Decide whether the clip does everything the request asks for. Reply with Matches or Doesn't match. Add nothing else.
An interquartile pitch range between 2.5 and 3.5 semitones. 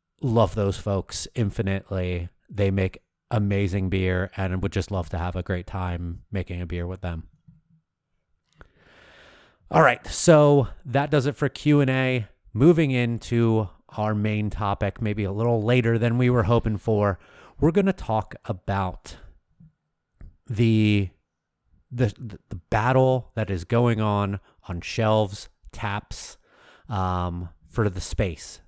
Doesn't match